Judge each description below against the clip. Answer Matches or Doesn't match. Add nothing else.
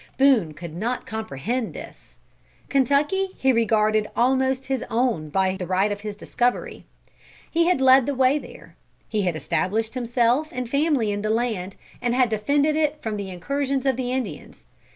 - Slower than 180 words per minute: Matches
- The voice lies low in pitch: Doesn't match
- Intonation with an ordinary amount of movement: Matches